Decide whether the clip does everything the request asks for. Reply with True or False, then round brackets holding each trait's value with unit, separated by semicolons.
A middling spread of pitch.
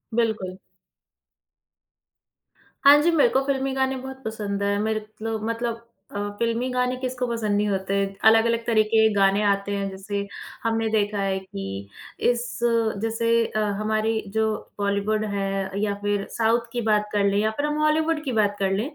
True (3.0 semitones)